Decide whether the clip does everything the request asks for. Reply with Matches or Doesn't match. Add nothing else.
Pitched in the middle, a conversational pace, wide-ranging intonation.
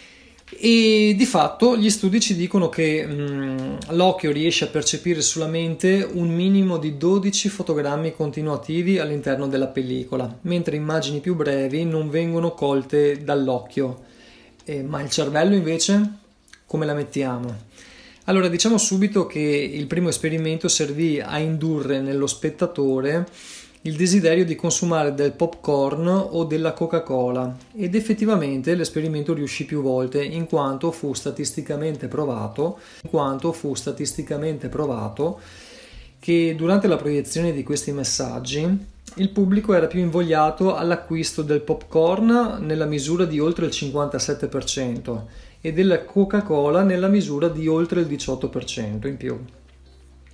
Doesn't match